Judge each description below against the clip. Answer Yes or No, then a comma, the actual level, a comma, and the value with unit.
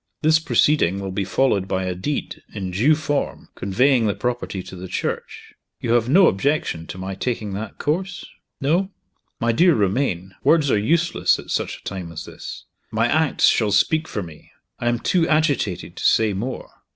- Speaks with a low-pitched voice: Yes, low, 115 Hz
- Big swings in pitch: Yes, wide, 7.6 semitones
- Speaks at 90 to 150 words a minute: No, average, 185 wpm